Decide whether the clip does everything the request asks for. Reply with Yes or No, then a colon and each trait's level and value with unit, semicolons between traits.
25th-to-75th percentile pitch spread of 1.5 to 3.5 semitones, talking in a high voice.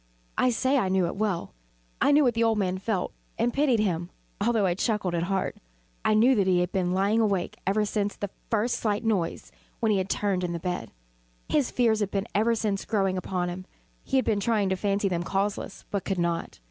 Yes: average, 3.2 semitones; high, 200 Hz